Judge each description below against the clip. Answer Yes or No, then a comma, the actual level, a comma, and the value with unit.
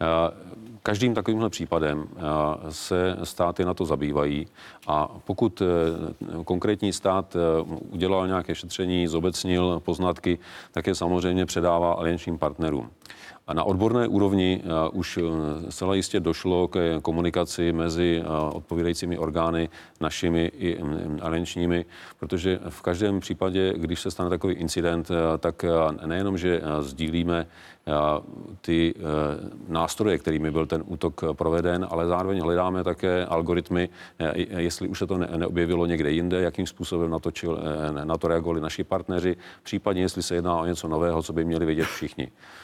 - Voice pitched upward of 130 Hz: No, very low, 85 Hz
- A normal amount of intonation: No, narrow, 1.8 semitones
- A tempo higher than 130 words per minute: No, average, 125 wpm